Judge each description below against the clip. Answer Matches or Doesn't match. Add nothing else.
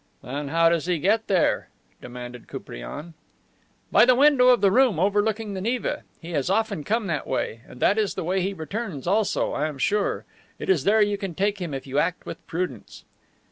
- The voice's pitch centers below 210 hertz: Matches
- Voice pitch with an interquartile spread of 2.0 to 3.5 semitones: Doesn't match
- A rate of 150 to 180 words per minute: Doesn't match